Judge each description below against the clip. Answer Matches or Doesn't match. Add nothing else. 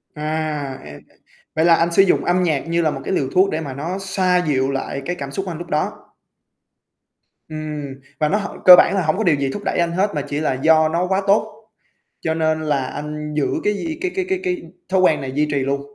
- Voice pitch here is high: Doesn't match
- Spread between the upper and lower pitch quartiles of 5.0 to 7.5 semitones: Doesn't match